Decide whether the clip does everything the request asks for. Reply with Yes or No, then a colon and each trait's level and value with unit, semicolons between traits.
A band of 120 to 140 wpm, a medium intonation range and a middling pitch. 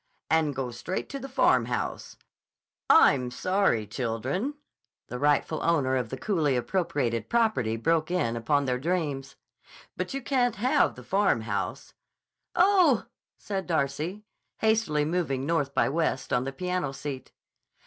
No: slow, 135 wpm; wide, 6.7 semitones; medium, 150 Hz